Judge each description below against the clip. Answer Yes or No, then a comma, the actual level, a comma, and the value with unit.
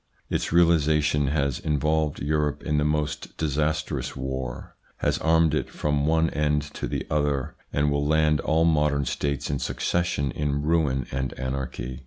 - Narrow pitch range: Yes, narrow, 1.6 semitones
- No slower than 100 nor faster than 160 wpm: Yes, average, 155 wpm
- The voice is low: Yes, very low, 75 Hz